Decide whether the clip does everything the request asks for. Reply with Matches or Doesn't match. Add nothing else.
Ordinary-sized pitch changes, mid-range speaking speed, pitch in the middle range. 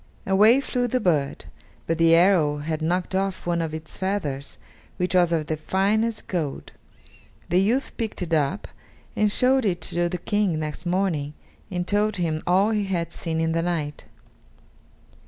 Matches